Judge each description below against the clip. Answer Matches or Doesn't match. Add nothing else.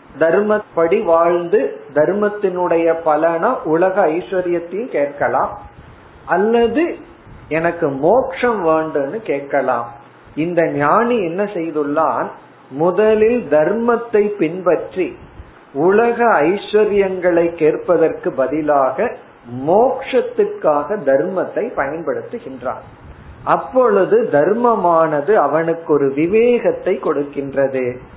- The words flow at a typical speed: Doesn't match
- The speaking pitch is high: Doesn't match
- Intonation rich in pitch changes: Matches